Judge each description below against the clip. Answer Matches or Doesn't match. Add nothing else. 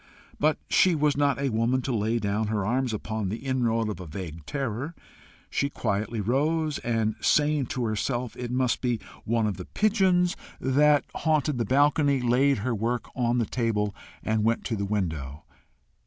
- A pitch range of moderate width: Matches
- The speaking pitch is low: Matches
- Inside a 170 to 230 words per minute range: Matches